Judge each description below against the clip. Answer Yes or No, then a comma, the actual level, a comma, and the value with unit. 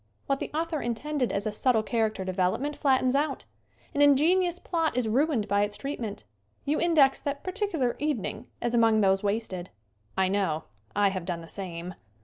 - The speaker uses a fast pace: No, average, 180 wpm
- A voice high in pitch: Yes, high, 235 Hz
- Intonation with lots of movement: Yes, wide, 6.4 semitones